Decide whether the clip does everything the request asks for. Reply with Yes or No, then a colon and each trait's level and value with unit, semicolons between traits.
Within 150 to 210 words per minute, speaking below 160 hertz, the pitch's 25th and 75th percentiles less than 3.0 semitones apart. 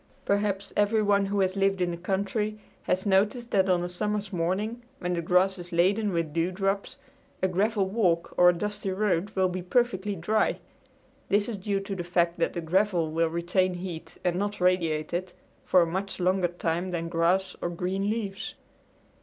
No: average, 185 wpm; medium, 185 Hz; narrow, 2.5 semitones